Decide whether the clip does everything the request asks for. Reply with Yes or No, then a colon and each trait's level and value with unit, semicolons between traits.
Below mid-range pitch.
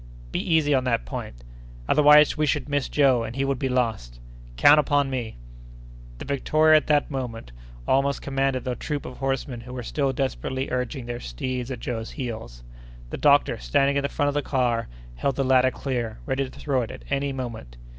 Yes: low, 130 Hz